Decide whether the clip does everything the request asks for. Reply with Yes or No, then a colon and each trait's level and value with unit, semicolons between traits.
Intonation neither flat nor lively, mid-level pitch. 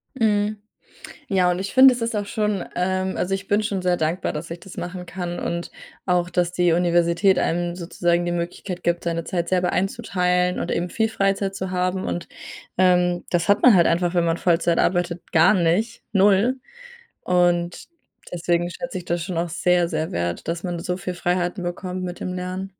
No: narrow, 1.7 semitones; medium, 180 Hz